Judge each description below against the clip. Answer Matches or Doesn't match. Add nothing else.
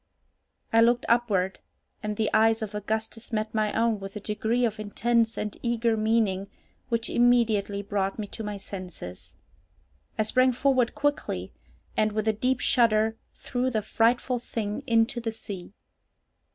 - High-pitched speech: Matches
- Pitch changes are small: Matches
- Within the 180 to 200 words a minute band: Doesn't match